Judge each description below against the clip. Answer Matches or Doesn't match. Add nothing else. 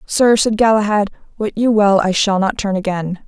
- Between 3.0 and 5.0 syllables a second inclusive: Matches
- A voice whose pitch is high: Matches